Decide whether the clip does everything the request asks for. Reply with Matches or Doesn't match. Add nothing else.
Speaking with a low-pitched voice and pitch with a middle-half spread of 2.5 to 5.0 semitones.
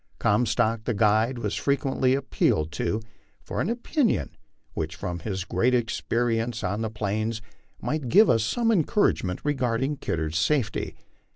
Matches